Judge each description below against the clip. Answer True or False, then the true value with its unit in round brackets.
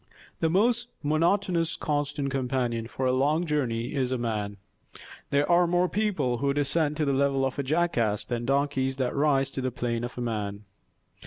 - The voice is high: False (140 Hz)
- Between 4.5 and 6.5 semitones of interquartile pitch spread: False (4.0 semitones)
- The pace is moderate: True (175 wpm)